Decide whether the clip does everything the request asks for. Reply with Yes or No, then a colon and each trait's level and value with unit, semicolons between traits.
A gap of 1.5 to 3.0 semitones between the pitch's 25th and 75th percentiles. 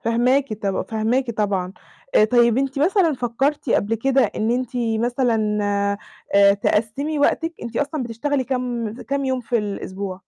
No: average, 3.7 semitones